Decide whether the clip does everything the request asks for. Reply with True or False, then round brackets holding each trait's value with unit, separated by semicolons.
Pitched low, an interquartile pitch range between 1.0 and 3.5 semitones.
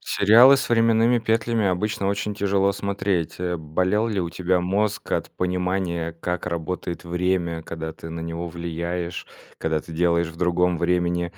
True (90 Hz; 2.8 semitones)